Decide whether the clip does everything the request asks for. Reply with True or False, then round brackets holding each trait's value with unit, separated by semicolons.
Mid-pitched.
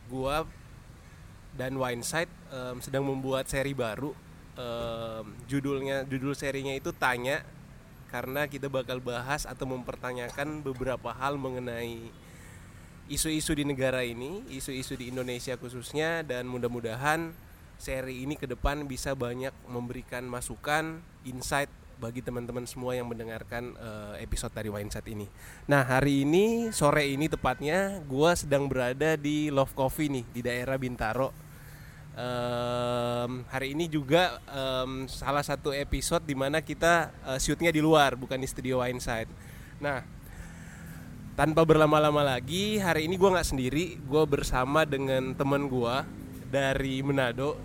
False (130 Hz)